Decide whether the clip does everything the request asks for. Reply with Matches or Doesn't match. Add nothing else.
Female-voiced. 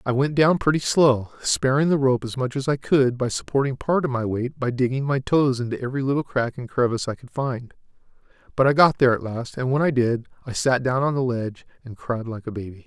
Doesn't match